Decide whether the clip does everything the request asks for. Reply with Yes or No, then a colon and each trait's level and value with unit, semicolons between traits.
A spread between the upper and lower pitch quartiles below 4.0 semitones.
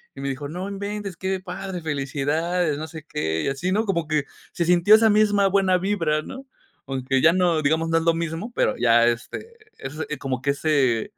No: average, 5.0 semitones